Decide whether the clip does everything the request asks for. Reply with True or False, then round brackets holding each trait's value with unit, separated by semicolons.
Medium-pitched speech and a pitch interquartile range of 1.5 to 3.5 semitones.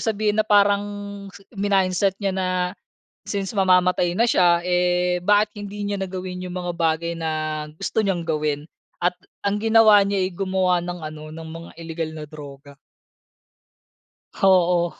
True (180 Hz; 3.2 semitones)